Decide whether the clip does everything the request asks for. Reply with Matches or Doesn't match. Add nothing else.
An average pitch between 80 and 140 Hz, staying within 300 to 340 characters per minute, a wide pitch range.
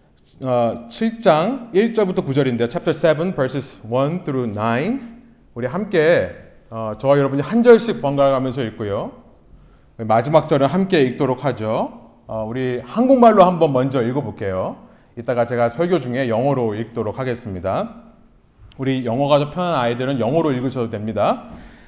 Matches